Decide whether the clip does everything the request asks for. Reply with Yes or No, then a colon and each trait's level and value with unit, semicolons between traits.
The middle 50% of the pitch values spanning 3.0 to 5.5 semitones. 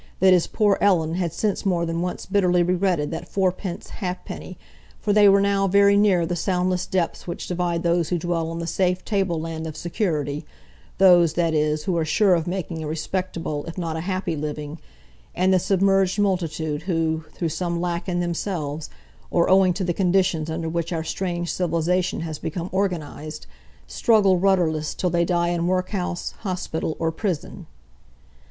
No: narrow, 2.4 semitones